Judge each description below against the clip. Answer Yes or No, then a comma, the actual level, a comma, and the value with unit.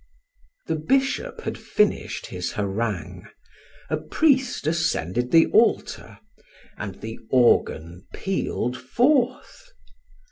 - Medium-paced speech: No, slow, 95 wpm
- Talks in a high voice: No, medium, 150 Hz